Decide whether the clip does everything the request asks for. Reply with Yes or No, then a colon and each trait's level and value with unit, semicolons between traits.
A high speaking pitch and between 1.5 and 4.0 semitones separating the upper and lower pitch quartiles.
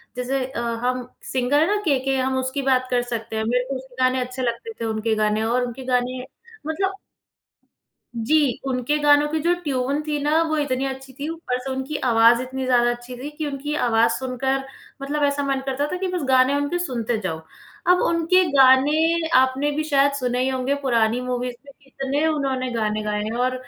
Yes: very high, 260 Hz; average, 2.7 semitones